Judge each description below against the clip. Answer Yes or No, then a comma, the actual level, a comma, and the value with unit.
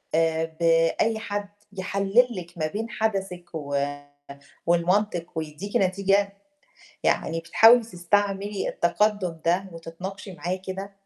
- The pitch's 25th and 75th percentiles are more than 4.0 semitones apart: No, average, 3.4 semitones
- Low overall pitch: No, high, 190 Hz